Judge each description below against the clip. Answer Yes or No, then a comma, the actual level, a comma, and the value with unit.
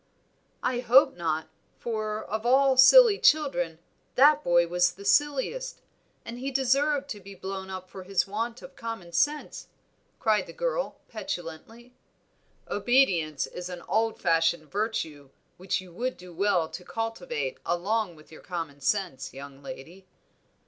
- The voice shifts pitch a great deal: Yes, wide, 6.4 semitones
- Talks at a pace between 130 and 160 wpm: Yes, average, 145 wpm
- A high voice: Yes, high, 200 Hz